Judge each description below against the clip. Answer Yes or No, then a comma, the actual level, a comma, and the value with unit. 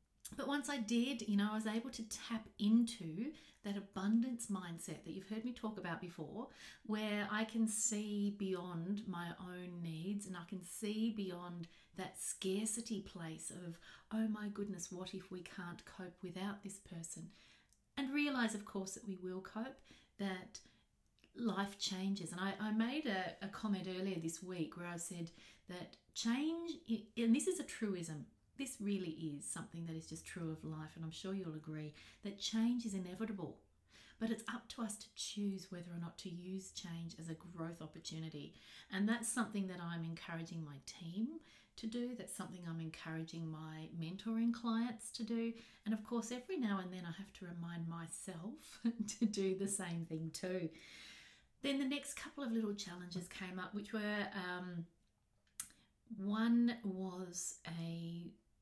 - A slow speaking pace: No, average, 175 wpm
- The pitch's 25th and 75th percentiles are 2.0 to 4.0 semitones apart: No, average, 4.4 semitones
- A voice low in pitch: No, high, 195 Hz